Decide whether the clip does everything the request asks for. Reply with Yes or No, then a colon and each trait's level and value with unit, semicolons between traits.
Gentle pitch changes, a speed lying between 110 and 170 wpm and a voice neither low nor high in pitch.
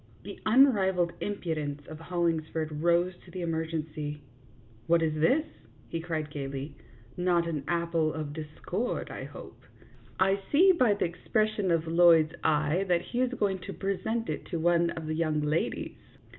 No: average, 3.4 semitones; average, 165 wpm; medium, 170 Hz